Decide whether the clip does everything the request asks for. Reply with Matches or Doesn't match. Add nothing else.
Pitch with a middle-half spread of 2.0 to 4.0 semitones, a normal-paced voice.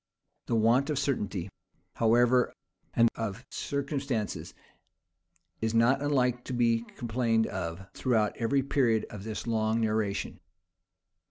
Doesn't match